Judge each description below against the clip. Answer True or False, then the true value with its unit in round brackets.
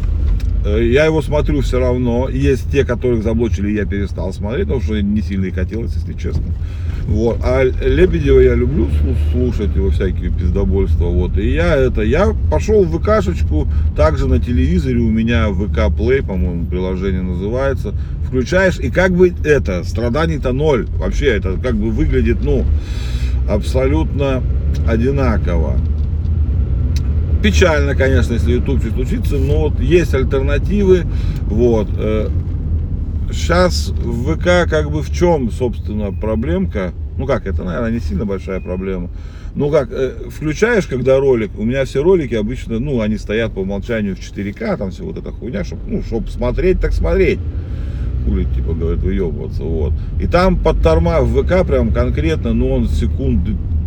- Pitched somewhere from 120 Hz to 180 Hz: False (85 Hz)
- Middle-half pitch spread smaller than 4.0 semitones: False (4.7 semitones)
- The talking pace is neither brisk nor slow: True (150 wpm)